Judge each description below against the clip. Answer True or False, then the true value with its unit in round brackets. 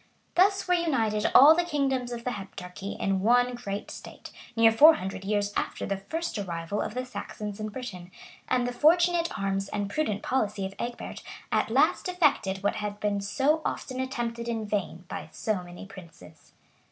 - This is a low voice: False (215 Hz)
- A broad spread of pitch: False (4.9 semitones)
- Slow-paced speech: False (175 wpm)